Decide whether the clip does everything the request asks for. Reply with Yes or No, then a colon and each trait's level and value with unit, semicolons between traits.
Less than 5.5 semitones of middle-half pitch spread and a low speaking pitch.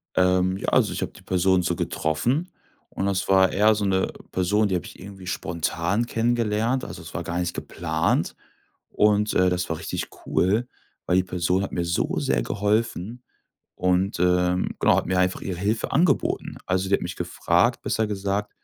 Yes: average, 2.8 semitones; very low, 95 Hz